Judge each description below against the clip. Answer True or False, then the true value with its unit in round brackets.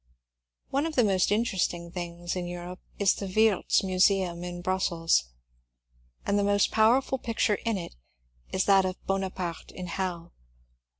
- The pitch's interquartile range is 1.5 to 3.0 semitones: True (2.5 semitones)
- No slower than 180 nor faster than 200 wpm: False (155 wpm)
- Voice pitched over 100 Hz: True (190 Hz)